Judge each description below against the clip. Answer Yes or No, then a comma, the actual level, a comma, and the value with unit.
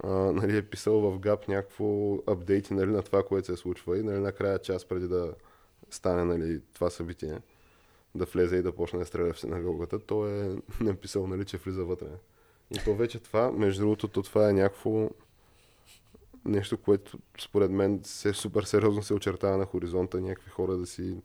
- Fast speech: Yes, fast, 180 wpm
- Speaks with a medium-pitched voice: No, low, 100 Hz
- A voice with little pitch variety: Yes, narrow, 2.2 semitones